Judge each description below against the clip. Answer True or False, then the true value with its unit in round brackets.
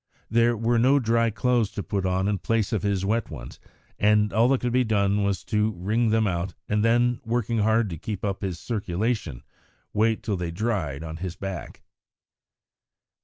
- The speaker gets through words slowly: False (185 wpm)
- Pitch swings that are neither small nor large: True (3.3 semitones)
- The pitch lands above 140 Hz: False (105 Hz)